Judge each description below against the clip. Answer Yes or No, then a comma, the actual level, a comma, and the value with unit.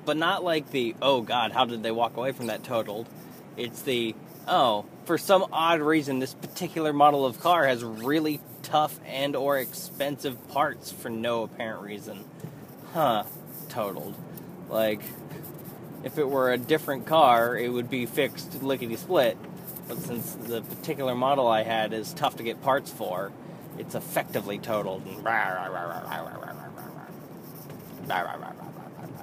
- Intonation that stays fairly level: No, average, 4.7 semitones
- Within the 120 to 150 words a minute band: Yes, average, 140 wpm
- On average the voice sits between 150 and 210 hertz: No, low, 135 Hz